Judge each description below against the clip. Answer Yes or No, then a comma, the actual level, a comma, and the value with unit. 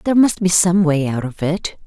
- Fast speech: Yes, fast, 255 wpm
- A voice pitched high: No, medium, 170 Hz